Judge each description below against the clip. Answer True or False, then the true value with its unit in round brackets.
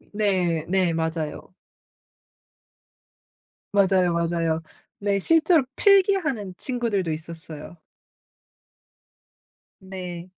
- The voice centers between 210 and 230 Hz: False (185 Hz)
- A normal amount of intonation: True (4.1 semitones)